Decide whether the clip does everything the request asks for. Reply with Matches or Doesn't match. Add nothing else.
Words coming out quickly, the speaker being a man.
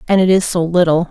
Doesn't match